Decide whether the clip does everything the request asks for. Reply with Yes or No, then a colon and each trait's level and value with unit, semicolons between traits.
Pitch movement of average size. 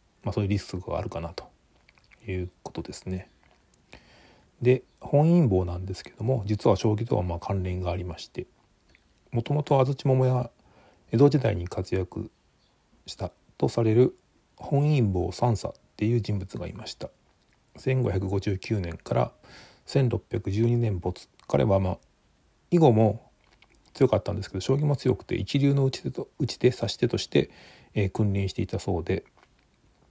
Yes: average, 5.0 semitones